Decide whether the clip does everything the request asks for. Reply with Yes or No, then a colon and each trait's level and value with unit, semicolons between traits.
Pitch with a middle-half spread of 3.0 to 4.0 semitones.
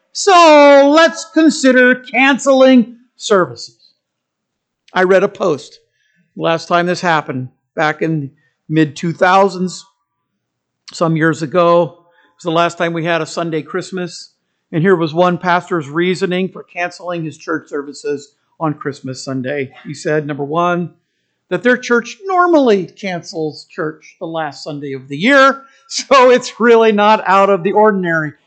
No: wide, 5.4 semitones